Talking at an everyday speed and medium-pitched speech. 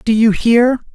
No: average, 190 wpm; high, 230 Hz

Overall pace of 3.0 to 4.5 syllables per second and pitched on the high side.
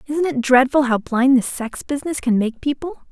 No: 5.2 syllables/s; very high, 265 Hz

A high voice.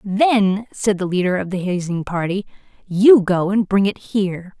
Yes: high, 195 Hz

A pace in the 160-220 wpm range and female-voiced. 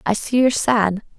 Yes: average, 200 wpm; female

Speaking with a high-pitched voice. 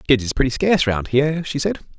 No: low, 130 Hz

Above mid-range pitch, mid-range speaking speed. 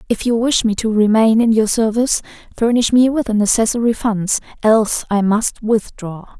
Yes: high, 220 Hz; average, 180 wpm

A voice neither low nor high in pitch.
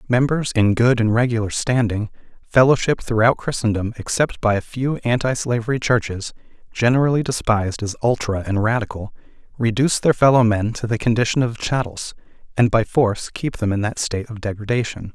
No: low, 115 Hz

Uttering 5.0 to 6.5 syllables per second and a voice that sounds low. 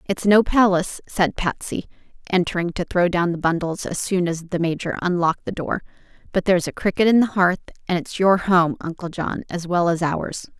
No: 5.3 syllables/s; medium, 180 Hz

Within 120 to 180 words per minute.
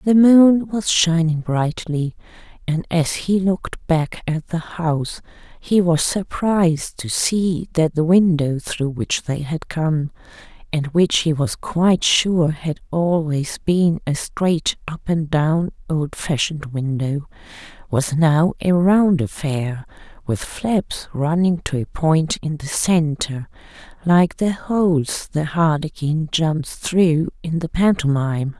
Yes: average, 140 wpm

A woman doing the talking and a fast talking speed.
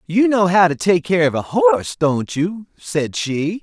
No: male; fast, 215 wpm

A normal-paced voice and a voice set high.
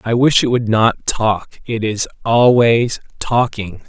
No: average, 155 wpm; low, 115 Hz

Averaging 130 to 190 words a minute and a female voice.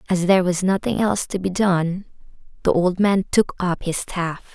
No: average, 200 wpm; female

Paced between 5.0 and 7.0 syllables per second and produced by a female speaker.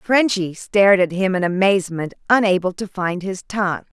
Yes: 5.2 syllables/s; female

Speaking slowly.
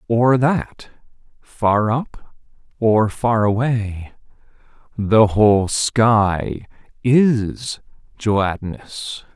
Yes: slow, 75 wpm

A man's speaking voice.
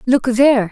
No: female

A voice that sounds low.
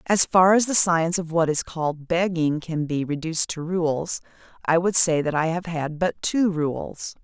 No: medium, 165 Hz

